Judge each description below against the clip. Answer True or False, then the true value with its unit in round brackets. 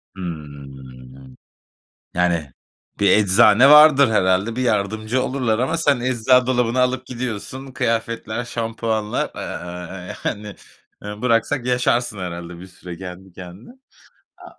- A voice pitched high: False (110 Hz)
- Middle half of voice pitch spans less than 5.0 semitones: False (5.6 semitones)